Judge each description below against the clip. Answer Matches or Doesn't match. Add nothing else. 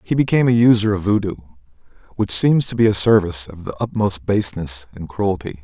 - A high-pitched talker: Doesn't match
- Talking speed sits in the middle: Matches